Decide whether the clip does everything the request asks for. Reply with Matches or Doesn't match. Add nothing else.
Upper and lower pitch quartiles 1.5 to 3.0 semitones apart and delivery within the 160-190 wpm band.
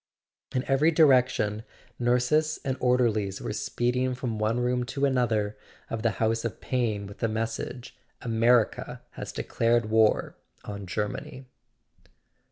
Doesn't match